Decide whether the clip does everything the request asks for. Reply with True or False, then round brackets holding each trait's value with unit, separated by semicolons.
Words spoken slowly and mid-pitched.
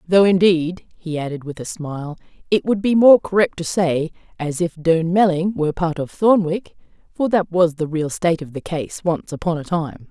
False (200 wpm; 170 Hz)